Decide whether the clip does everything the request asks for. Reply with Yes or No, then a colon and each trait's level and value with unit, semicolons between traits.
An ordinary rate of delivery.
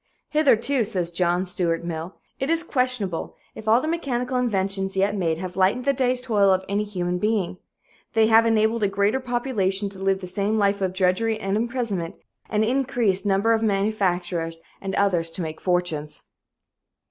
Yes: average, 175 wpm